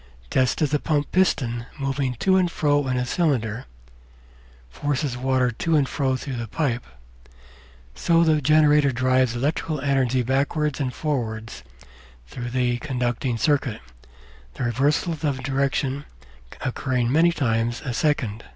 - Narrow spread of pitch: No, average, 3.2 semitones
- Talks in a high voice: No, low, 135 Hz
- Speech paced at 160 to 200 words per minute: No, slow, 135 wpm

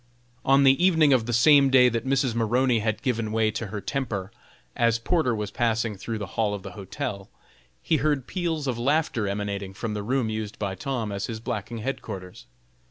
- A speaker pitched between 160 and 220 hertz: No, low, 115 Hz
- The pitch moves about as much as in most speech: Yes, average, 4.4 semitones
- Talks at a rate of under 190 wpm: No, average, 195 wpm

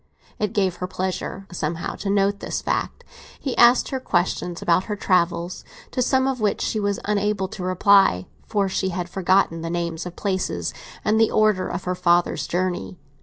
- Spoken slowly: No, average, 180 wpm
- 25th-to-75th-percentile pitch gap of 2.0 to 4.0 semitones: Yes, average, 2.9 semitones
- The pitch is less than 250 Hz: Yes, high, 190 Hz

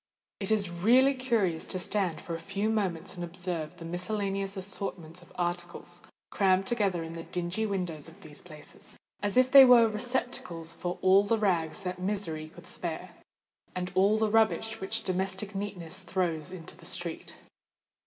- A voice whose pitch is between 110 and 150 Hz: No, medium, 185 Hz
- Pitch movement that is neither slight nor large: Yes, average, 3.1 semitones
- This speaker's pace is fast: No, average, 165 wpm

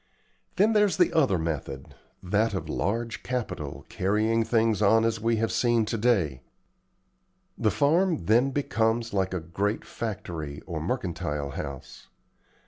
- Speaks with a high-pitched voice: No, low, 110 Hz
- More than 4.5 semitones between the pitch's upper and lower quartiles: Yes, wide, 5.4 semitones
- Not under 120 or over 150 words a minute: Yes, slow, 135 wpm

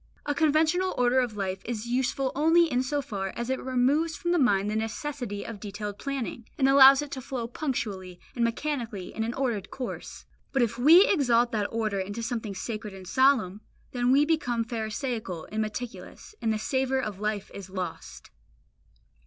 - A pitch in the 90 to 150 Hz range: No, high, 240 Hz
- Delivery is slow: No, average, 180 wpm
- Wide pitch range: No, average, 4.2 semitones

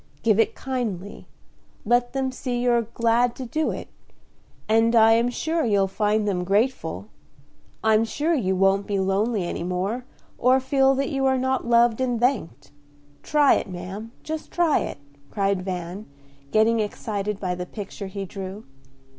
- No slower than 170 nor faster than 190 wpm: No, average, 160 wpm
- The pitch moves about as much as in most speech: Yes, average, 4.4 semitones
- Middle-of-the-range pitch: No, high, 225 Hz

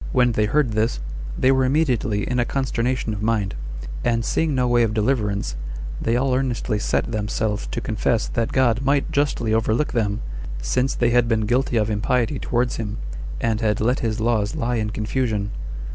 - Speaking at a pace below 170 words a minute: No, average, 180 wpm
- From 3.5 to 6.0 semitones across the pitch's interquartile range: No, average, 2.9 semitones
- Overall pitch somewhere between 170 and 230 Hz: No, low, 115 Hz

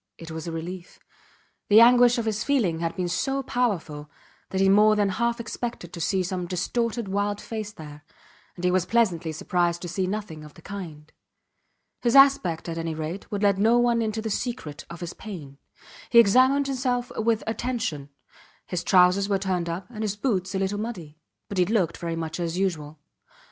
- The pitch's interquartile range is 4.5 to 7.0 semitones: Yes, average, 5.0 semitones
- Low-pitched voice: No, high, 195 Hz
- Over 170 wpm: Yes, average, 190 wpm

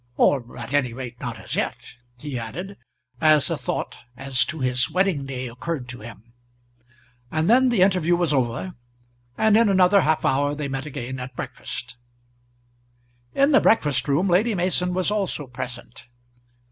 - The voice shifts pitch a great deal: Yes, wide, 6.4 semitones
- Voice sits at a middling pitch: Yes, medium, 145 Hz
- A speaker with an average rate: Yes, average, 160 wpm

